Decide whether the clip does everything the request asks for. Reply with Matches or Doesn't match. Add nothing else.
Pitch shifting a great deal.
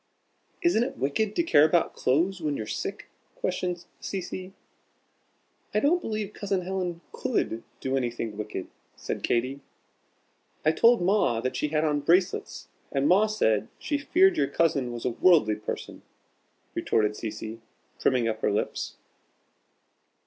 Matches